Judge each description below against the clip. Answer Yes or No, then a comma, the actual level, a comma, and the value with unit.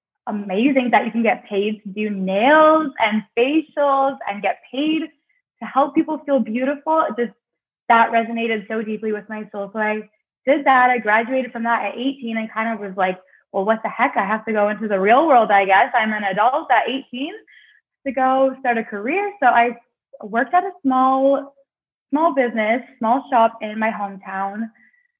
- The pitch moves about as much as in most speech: Yes, average, 4.1 semitones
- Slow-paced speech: No, average, 190 wpm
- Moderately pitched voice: No, high, 235 Hz